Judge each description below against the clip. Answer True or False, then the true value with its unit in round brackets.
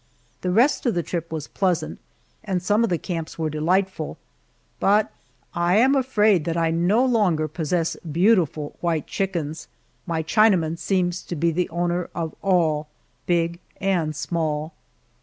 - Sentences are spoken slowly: False (150 wpm)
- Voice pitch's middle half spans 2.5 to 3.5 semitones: True (3.1 semitones)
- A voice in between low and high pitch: True (175 Hz)